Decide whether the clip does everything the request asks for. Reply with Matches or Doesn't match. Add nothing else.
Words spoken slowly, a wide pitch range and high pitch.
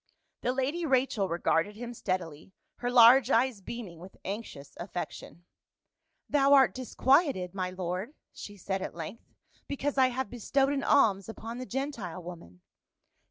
Doesn't match